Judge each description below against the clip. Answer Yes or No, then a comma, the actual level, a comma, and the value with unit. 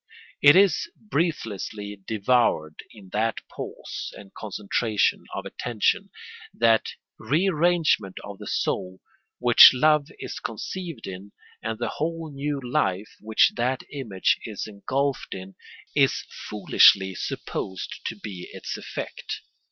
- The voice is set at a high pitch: No, low, 115 Hz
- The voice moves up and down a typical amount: No, wide, 6.2 semitones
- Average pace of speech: No, slow, 120 wpm